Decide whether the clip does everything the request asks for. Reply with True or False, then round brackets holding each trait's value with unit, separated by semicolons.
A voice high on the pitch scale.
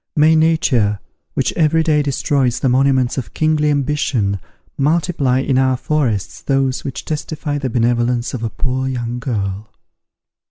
False (130 Hz)